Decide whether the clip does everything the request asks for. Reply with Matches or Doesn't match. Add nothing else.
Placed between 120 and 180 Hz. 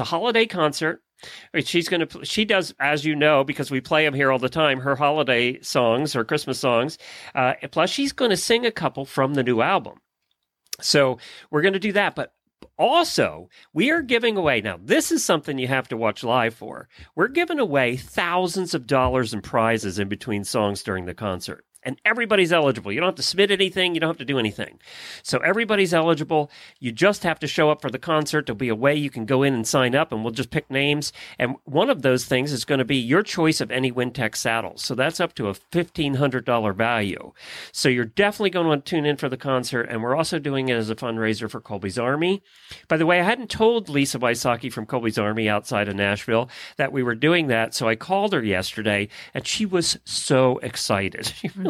Matches